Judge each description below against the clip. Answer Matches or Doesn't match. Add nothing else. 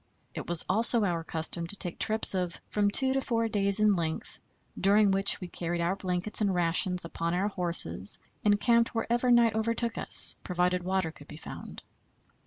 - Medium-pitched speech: Doesn't match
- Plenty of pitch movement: Doesn't match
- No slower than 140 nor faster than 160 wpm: Doesn't match